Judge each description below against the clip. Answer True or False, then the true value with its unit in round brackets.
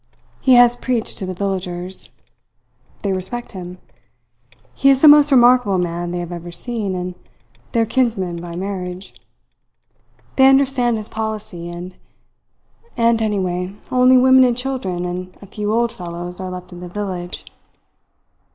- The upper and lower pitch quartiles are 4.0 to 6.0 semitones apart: True (5.2 semitones)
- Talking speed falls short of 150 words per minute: True (140 wpm)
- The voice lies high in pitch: True (195 Hz)